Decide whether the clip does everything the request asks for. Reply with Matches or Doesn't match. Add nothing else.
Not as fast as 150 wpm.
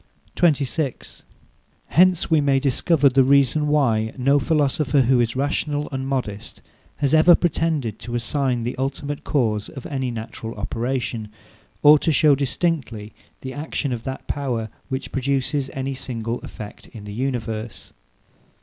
Matches